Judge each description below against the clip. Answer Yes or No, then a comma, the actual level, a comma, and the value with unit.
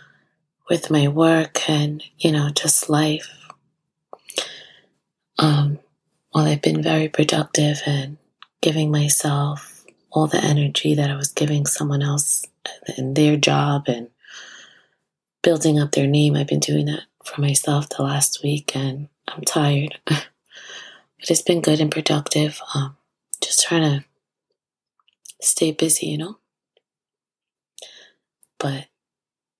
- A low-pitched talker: No, medium, 150 Hz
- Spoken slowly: Yes, slow, 125 wpm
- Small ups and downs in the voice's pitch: Yes, narrow, 1.5 semitones